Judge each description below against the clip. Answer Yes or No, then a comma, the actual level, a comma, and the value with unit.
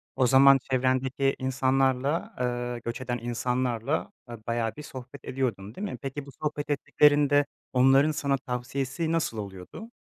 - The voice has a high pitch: No, low, 130 Hz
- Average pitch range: No, narrow, 2.3 semitones